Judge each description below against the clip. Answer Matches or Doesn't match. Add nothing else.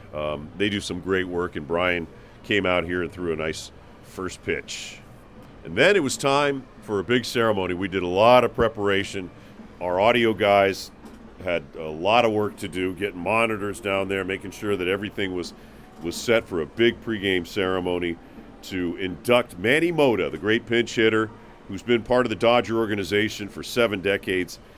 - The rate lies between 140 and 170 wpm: Doesn't match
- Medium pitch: Doesn't match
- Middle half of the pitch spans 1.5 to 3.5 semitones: Doesn't match